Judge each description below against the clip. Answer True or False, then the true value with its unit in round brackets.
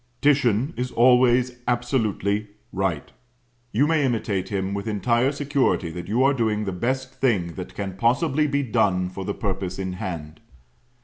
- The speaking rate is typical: True (160 wpm)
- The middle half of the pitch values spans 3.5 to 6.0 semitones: True (5.2 semitones)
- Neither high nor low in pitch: False (115 Hz)